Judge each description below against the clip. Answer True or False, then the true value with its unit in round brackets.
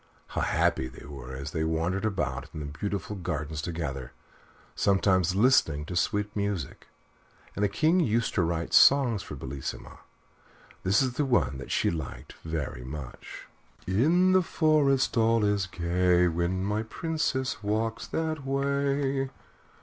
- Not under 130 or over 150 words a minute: True (140 wpm)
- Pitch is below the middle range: True (95 Hz)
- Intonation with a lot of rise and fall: True (8.6 semitones)